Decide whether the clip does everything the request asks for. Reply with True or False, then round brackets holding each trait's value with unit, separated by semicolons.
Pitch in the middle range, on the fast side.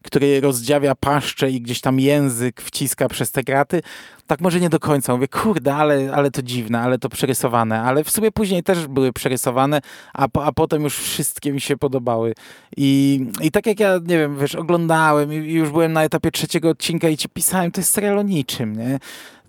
True (145 Hz; 200 wpm)